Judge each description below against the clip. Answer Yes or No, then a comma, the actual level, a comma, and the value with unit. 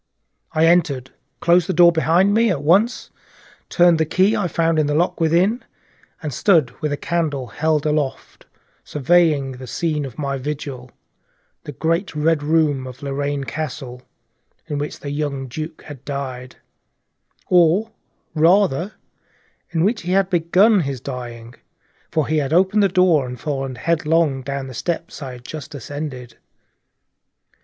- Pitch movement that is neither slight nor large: Yes, average, 3.8 semitones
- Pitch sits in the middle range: Yes, medium, 155 Hz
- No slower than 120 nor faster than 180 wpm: Yes, average, 150 wpm